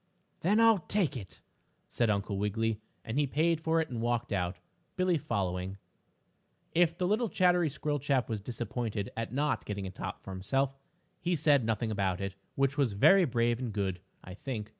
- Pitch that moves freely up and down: Yes, wide, 7.5 semitones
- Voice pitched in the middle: No, low, 120 Hz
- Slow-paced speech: No, average, 180 wpm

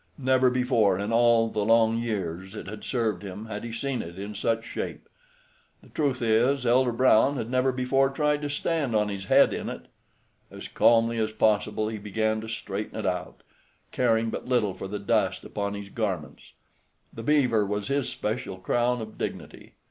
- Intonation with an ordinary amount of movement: Yes, average, 3.4 semitones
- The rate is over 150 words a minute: Yes, average, 185 wpm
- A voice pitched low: Yes, low, 115 Hz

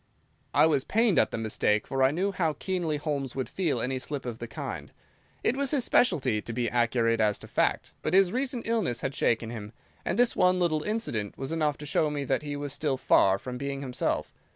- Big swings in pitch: Yes, wide, 6.6 semitones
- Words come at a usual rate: No, fast, 225 wpm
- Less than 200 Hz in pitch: Yes, medium, 140 Hz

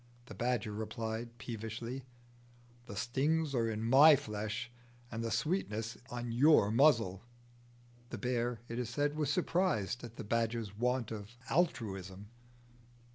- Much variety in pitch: No, average, 2.9 semitones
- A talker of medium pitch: No, low, 115 Hz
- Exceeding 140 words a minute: No, slow, 135 wpm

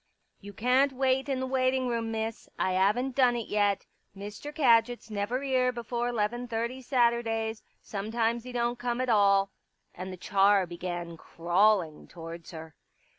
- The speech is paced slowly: No, average, 160 wpm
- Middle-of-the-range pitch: No, high, 225 Hz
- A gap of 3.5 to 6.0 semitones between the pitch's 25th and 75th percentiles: Yes, average, 3.9 semitones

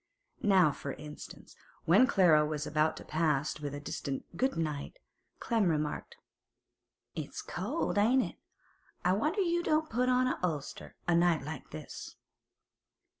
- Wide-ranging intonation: Yes, wide, 8.8 semitones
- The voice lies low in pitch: No, medium, 170 Hz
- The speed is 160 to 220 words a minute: No, average, 145 wpm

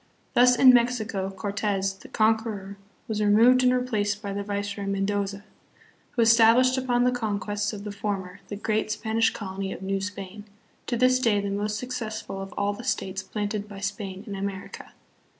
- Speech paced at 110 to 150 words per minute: No, average, 175 wpm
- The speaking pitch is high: Yes, high, 205 Hz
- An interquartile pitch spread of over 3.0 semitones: No, narrow, 2.4 semitones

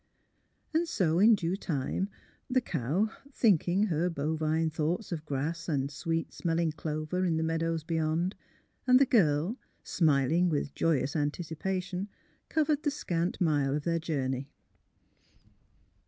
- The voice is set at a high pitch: No, medium, 165 Hz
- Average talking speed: No, slow, 130 wpm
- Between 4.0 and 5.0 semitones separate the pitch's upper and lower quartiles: No, average, 3.4 semitones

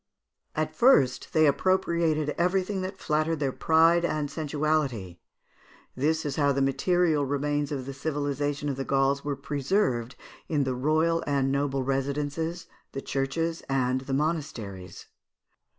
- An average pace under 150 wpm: Yes, slow, 135 wpm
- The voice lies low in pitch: No, medium, 145 Hz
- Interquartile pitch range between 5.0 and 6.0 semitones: No, average, 2.8 semitones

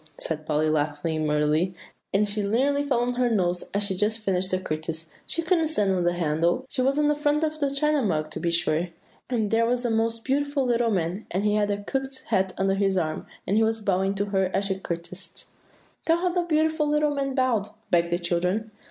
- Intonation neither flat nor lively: No, wide, 7.1 semitones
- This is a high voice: Yes, high, 205 Hz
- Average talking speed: No, fast, 230 wpm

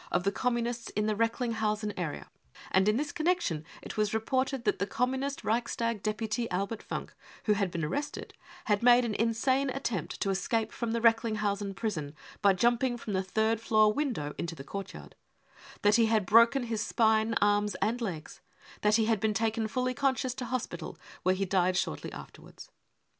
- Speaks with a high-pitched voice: Yes, high, 220 Hz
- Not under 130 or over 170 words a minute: No, average, 180 wpm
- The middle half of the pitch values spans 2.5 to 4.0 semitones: Yes, average, 2.9 semitones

